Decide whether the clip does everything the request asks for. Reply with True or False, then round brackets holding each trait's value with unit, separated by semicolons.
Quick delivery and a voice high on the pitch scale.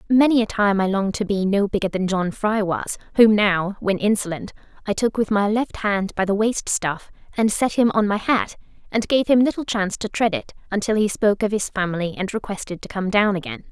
True (230 wpm; 205 Hz)